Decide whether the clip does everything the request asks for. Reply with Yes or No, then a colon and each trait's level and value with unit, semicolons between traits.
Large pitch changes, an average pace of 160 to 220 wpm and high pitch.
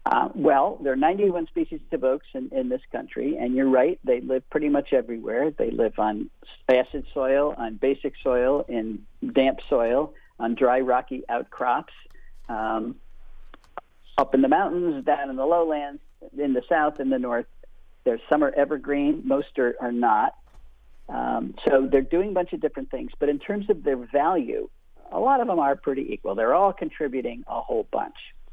No: wide, 5.8 semitones; average, 180 wpm; medium, 140 Hz